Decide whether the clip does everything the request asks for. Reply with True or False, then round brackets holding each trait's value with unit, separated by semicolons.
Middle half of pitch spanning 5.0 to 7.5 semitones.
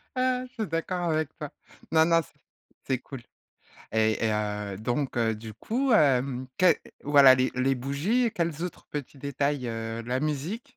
True (5.4 semitones)